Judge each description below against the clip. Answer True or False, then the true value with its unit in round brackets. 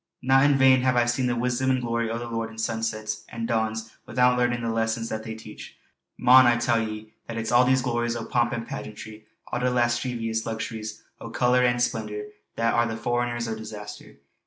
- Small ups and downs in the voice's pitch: True (1.6 semitones)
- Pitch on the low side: True (115 Hz)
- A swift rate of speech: True (210 wpm)